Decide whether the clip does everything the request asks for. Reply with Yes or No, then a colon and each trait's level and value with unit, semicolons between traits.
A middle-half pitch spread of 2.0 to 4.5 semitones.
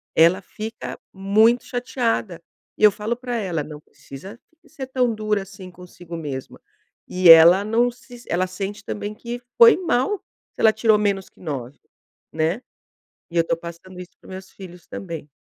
No: average, 5.0 semitones